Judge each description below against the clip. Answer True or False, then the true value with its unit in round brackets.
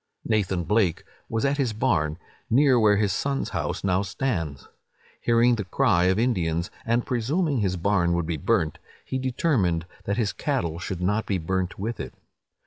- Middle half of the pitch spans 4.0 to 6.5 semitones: True (5.2 semitones)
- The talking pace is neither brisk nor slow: True (170 wpm)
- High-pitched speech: False (105 Hz)